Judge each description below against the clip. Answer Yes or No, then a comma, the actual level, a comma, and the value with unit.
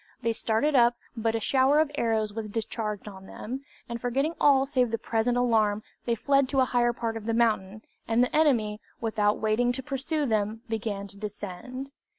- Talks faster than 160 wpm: Yes, average, 190 wpm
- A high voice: Yes, high, 230 Hz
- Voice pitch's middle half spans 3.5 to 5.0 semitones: No, average, 3.1 semitones